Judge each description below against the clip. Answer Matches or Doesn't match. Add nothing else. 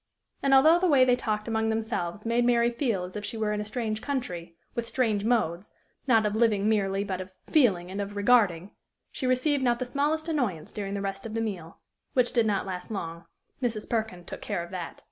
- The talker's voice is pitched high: Matches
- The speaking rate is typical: Doesn't match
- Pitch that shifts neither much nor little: Matches